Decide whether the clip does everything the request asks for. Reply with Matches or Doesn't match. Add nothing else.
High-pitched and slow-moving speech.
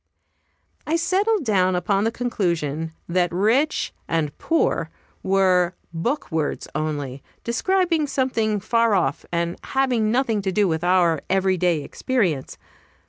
Matches